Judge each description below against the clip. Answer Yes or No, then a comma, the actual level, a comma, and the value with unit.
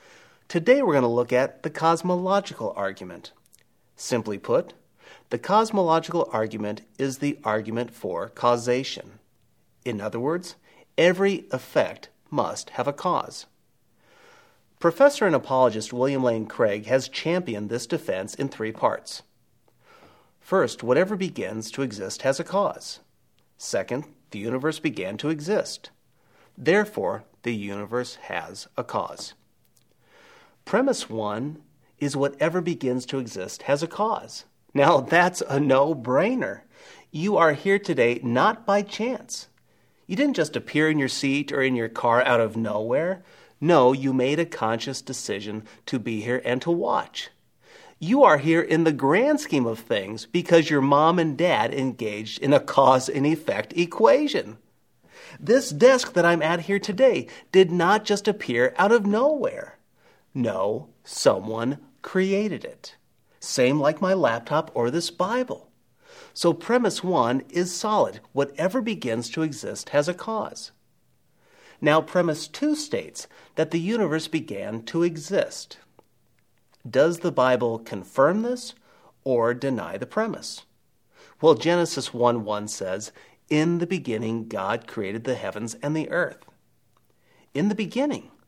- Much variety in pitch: Yes, wide, 7.7 semitones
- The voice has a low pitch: No, medium, 155 Hz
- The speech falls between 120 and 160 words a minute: Yes, average, 140 wpm